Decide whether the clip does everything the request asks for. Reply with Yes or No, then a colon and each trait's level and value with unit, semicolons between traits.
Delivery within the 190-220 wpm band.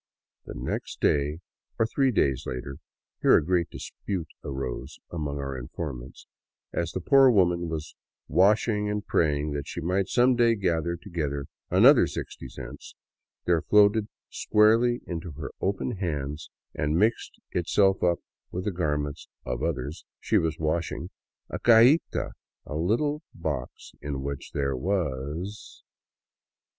No: average, 150 wpm